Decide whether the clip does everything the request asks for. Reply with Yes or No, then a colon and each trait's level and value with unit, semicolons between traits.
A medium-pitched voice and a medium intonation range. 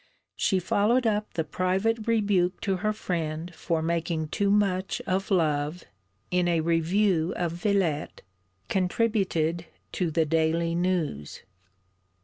Yes: medium, 180 Hz; average, 3.4 semitones